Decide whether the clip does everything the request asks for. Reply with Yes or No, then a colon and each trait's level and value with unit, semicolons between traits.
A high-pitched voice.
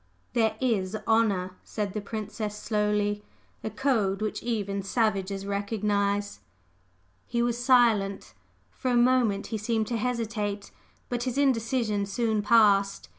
Yes: high, 215 Hz